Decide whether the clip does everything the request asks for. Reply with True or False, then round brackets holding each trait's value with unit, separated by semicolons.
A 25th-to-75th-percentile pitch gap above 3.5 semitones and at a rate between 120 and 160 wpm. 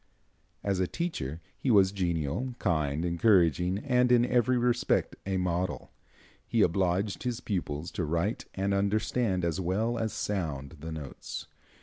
True (5.0 semitones; 140 wpm)